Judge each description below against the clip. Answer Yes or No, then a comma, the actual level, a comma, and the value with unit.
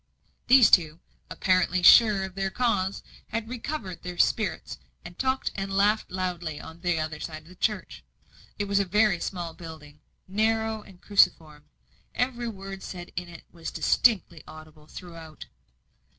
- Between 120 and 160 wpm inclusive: Yes, average, 150 wpm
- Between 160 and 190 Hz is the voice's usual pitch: Yes, medium, 185 Hz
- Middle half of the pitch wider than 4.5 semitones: No, average, 4.1 semitones